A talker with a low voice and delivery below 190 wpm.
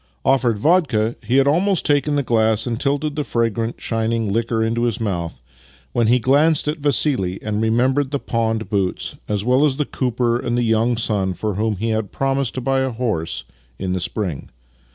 No: low, 115 Hz; average, 195 wpm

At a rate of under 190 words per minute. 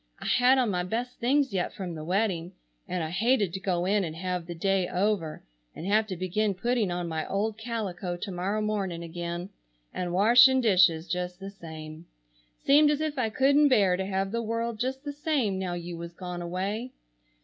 No: average, 200 wpm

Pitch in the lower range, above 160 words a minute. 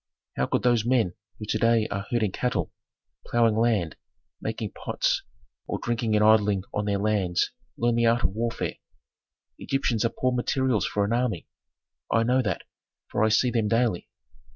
Yes: low, 115 Hz; average, 170 wpm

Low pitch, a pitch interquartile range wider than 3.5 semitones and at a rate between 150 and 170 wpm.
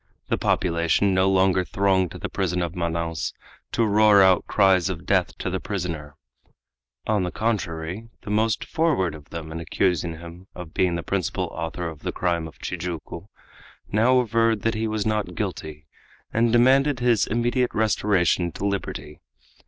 Yes: very low, 95 Hz; average, 4.3 semitones; average, 165 wpm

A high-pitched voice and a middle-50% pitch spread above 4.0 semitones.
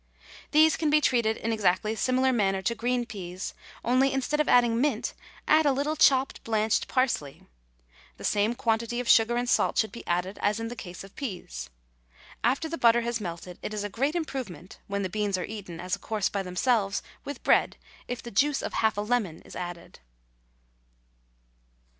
Yes: high, 225 Hz; average, 4.5 semitones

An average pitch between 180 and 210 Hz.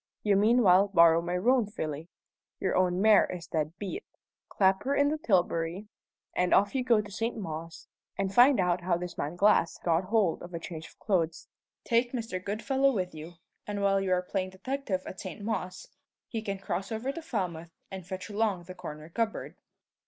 Yes: high, 190 Hz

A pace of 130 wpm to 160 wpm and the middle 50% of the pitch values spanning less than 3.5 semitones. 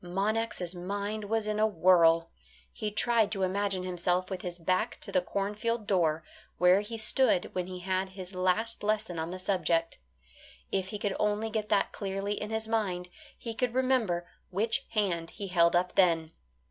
No: average, 175 wpm; average, 3.1 semitones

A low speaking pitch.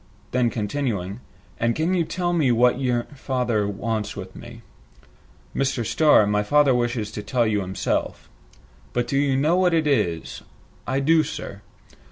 Yes: low, 125 Hz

